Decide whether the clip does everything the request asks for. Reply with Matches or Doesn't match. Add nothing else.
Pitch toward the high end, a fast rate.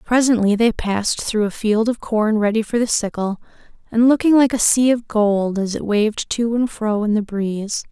Matches